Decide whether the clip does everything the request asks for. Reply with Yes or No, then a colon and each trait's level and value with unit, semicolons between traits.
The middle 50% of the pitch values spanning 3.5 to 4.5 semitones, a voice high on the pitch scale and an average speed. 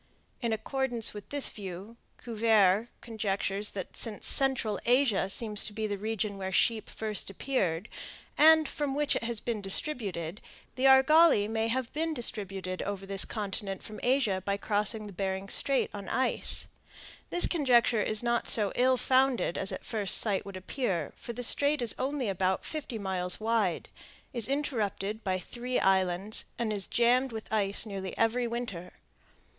Yes: average, 4.1 semitones; high, 220 Hz; average, 160 wpm